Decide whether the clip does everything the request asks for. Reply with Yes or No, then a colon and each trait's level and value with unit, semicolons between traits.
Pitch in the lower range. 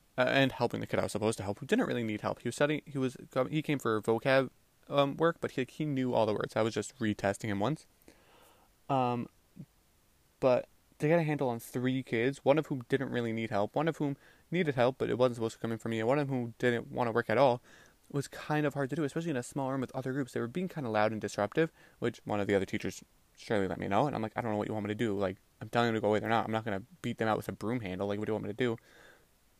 Yes: low, 120 Hz